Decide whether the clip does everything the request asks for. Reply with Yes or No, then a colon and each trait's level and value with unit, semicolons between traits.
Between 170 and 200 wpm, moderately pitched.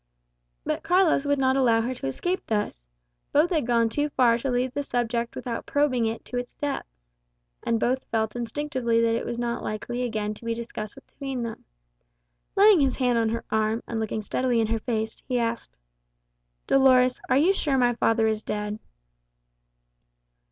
No: average, 180 wpm; high, 240 Hz